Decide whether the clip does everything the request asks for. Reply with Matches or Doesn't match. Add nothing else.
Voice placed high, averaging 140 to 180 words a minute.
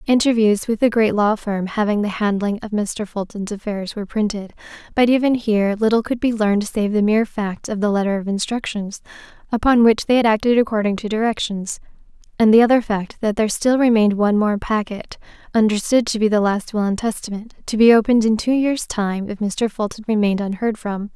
Doesn't match